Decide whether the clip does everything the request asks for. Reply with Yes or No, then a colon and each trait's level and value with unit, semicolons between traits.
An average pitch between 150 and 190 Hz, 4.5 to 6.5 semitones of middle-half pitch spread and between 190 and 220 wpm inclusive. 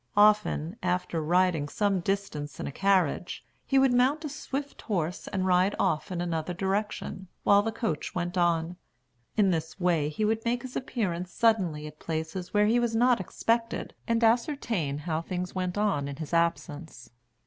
No: medium, 185 Hz; average, 5.0 semitones; average, 170 wpm